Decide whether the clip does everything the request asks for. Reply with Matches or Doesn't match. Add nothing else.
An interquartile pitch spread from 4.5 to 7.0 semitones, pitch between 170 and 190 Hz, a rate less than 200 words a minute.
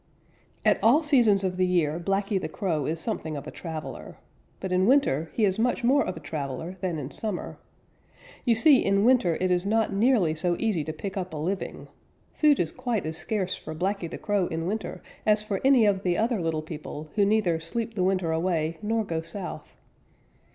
Doesn't match